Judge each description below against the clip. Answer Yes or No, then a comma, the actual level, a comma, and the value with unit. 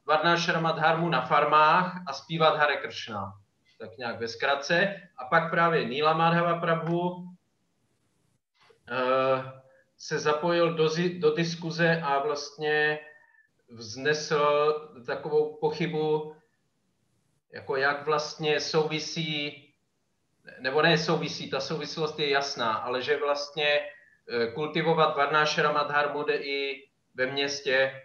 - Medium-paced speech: No, slow, 105 wpm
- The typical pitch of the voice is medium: Yes, medium, 150 Hz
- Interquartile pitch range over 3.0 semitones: No, narrow, 2.6 semitones